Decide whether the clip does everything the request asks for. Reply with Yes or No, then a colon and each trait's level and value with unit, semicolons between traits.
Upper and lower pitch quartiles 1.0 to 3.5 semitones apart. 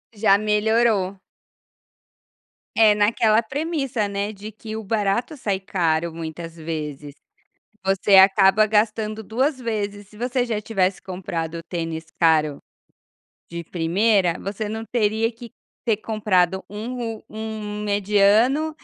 Yes: average, 2.8 semitones